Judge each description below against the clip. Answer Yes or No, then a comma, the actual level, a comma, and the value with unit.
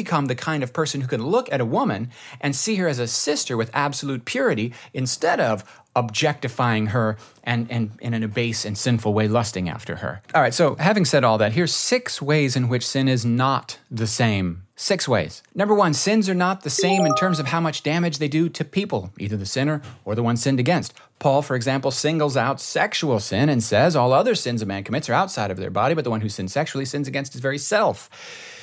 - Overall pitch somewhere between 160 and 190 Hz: No, low, 135 Hz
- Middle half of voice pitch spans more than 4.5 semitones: Yes, average, 5.1 semitones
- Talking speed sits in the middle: No, fast, 235 wpm